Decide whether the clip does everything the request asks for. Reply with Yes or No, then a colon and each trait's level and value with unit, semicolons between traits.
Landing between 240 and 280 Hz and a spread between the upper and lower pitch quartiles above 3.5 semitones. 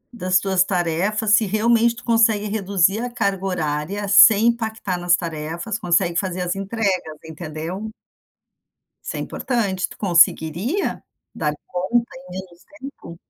No: high, 195 Hz; average, 4.0 semitones